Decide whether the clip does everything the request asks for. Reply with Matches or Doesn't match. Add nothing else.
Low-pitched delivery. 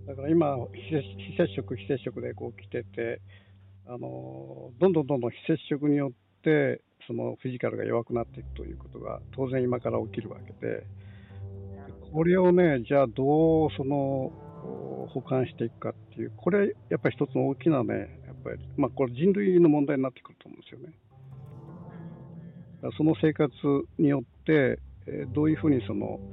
Matches